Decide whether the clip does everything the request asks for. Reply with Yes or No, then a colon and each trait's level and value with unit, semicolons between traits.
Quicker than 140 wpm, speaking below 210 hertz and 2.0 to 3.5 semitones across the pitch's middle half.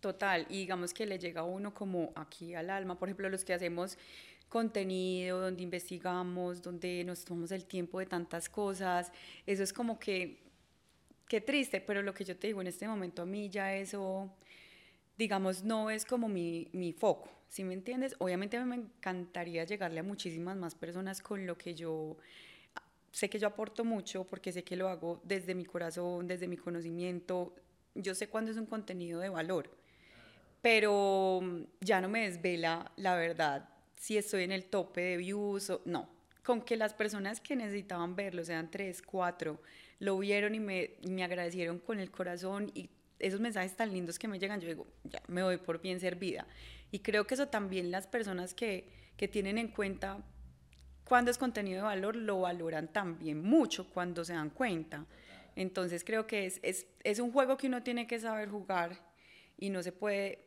Yes: fast, 190 wpm; high, 190 Hz; average, 2.7 semitones